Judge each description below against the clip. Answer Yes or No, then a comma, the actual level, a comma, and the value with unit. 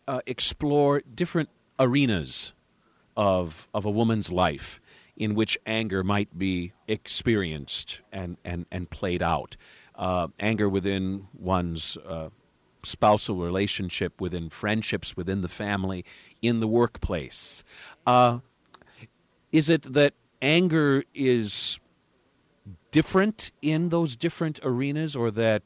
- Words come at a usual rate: No, slow, 115 wpm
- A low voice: Yes, low, 105 Hz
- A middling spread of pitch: No, wide, 5.9 semitones